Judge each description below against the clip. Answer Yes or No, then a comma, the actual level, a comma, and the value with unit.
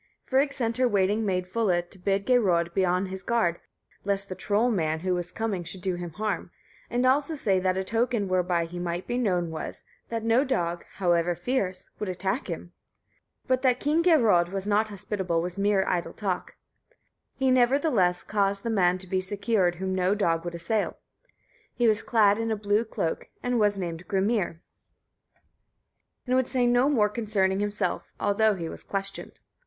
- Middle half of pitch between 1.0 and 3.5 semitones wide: No, average, 4.1 semitones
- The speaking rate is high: No, average, 180 wpm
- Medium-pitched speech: No, high, 200 Hz